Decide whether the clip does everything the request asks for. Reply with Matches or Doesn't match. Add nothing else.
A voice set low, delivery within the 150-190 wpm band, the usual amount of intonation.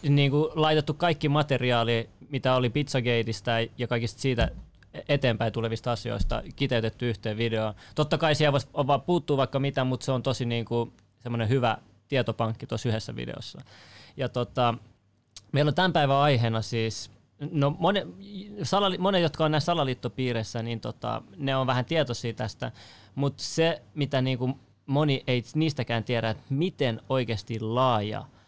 Matches